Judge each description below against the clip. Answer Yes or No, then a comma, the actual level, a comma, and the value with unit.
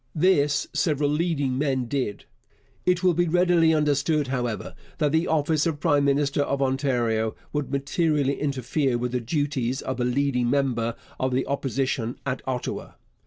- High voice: No, medium, 140 Hz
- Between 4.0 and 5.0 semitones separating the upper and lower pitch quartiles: No, average, 2.8 semitones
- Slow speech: No, average, 155 wpm